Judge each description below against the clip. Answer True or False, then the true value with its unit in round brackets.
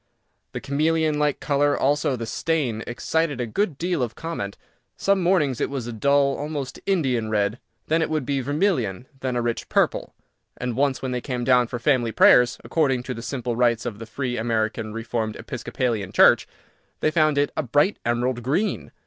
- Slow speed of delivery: False (190 wpm)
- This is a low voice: True (130 Hz)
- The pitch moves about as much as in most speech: True (4.0 semitones)